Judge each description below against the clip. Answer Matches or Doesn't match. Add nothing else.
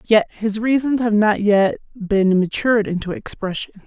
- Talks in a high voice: Matches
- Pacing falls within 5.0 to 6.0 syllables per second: Doesn't match